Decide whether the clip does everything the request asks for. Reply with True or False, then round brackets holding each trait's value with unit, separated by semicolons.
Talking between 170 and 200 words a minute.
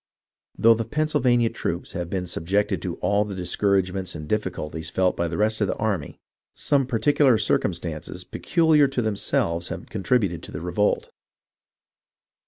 False (155 wpm)